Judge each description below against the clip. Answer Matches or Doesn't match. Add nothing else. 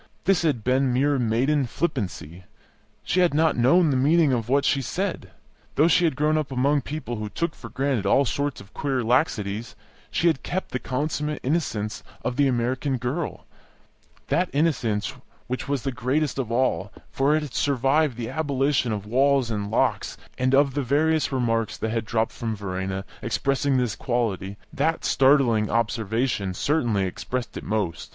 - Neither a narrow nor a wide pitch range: Matches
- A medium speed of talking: Matches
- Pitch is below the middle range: Matches